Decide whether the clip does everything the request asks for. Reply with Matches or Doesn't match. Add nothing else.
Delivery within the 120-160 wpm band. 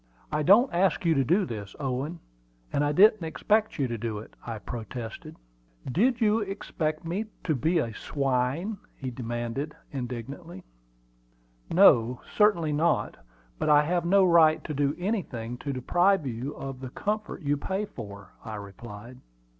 Matches